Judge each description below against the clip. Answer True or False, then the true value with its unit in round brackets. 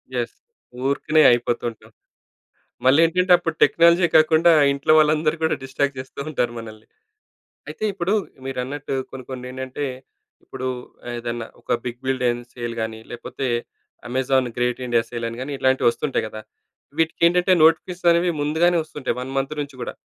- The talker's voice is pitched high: False (135 Hz)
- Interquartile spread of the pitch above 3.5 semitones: True (4.5 semitones)